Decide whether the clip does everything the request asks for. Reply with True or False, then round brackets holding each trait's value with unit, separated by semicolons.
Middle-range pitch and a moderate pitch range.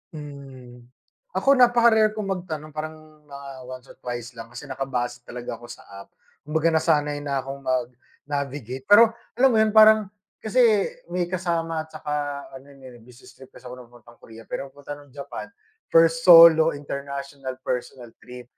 True (145 Hz; 4.4 semitones)